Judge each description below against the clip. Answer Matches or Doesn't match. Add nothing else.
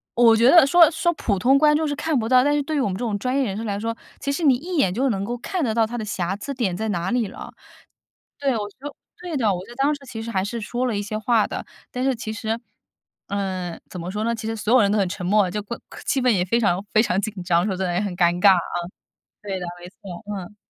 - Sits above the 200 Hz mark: Matches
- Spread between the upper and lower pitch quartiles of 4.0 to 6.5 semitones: Matches